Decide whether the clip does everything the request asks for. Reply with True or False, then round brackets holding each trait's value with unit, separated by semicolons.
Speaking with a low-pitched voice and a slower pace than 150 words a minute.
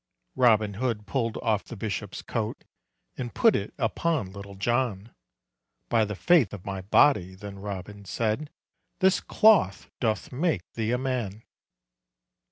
True (110 Hz; 140 wpm)